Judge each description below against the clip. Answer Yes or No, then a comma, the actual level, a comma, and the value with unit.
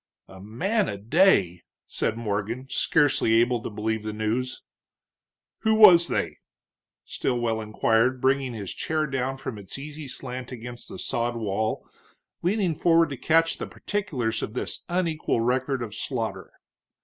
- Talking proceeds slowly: No, average, 145 wpm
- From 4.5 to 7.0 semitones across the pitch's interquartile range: Yes, wide, 5.6 semitones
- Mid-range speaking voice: No, low, 125 Hz